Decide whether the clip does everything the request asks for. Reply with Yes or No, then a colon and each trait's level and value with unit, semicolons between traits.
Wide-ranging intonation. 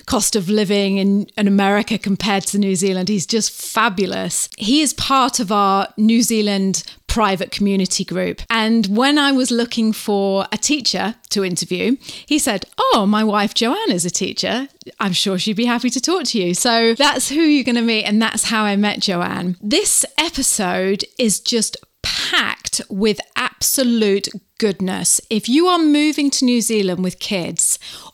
No: average, 3.7 semitones